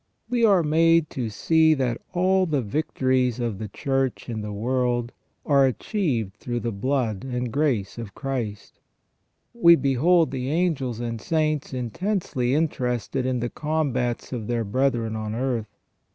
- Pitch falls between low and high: No, low, 130 Hz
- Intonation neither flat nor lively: Yes, average, 4.7 semitones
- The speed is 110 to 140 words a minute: No, average, 150 wpm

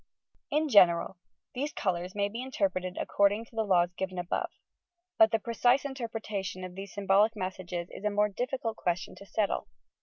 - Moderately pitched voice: No, high, 200 Hz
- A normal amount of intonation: Yes, average, 3.4 semitones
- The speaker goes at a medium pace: Yes, average, 185 wpm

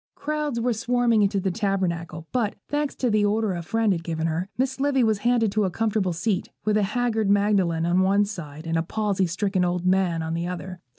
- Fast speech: Yes, fast, 220 wpm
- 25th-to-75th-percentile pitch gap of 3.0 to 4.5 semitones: Yes, average, 4.2 semitones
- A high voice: Yes, high, 200 Hz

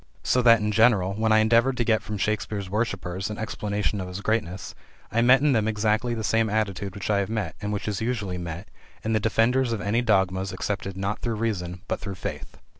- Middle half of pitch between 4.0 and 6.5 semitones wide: No, narrow, 2.6 semitones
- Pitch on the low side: Yes, low, 105 Hz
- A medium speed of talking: No, fast, 220 wpm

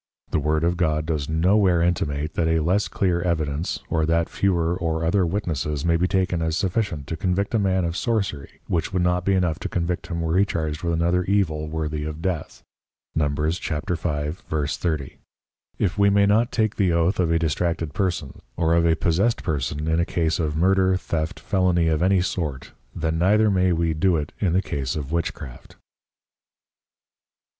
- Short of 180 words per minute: No, average, 185 wpm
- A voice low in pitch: Yes, very low, 85 Hz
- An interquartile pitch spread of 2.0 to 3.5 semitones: Yes, average, 2.9 semitones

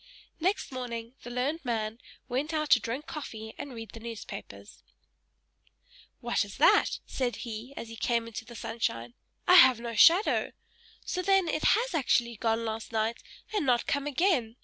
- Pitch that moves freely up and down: No, average, 4.8 semitones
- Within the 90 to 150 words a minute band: No, average, 170 wpm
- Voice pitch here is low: No, high, 240 Hz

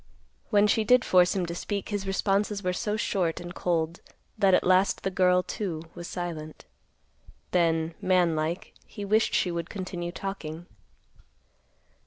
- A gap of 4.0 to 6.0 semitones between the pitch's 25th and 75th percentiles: No, narrow, 2.6 semitones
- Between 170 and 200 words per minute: No, average, 155 wpm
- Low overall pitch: No, medium, 180 Hz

